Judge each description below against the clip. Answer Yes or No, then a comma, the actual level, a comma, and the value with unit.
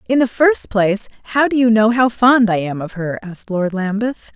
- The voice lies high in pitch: Yes, high, 220 Hz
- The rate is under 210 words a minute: No, fast, 235 wpm